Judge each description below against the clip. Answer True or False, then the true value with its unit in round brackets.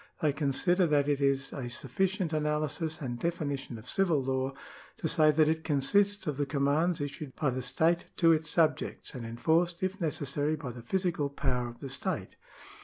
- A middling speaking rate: True (180 wpm)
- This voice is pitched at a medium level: True (150 Hz)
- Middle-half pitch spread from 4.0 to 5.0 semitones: False (3.4 semitones)